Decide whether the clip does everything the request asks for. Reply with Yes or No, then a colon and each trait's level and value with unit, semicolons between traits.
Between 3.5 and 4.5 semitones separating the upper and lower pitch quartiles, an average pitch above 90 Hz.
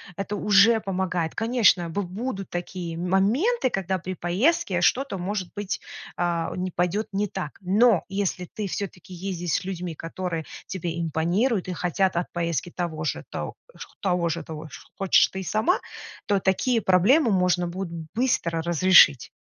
No: average, 2.9 semitones; medium, 185 Hz